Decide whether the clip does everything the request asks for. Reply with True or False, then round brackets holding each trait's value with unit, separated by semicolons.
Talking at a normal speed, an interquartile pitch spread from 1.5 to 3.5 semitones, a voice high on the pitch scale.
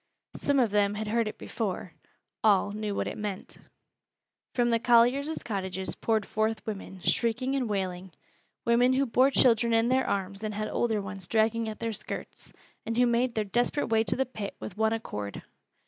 True (185 wpm; 2.7 semitones; 220 Hz)